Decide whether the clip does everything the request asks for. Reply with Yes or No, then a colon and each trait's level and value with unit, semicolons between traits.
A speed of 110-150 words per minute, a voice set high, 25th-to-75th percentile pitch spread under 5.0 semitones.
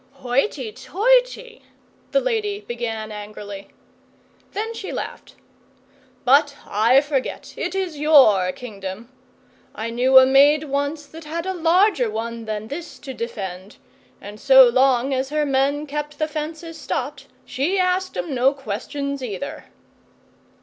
No: slow, 135 wpm; very high, 275 Hz; wide, 5.4 semitones